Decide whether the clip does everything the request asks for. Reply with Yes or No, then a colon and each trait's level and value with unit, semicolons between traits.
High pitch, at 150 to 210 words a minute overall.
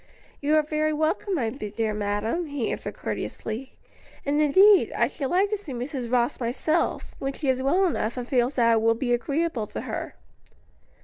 Yes: very high, 270 Hz; average, 185 wpm